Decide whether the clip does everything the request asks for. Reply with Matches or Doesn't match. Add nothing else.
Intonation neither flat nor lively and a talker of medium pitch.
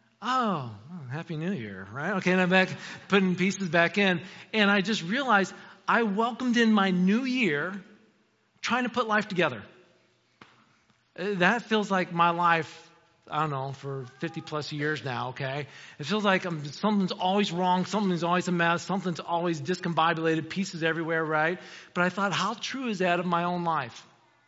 Matches